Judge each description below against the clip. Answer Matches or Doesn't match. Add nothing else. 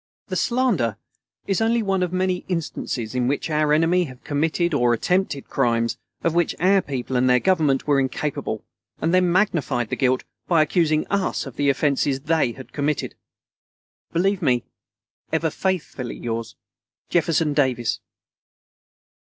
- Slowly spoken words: Doesn't match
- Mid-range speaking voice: Matches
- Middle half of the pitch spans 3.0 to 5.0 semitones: Doesn't match